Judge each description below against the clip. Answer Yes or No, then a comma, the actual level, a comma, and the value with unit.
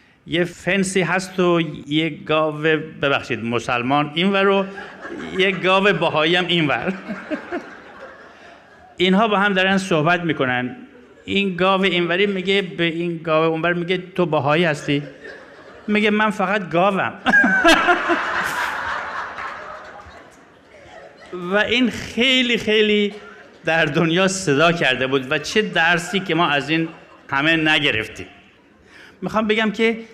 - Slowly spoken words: No, average, 115 wpm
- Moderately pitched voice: Yes, medium, 180 Hz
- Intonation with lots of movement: No, average, 4.0 semitones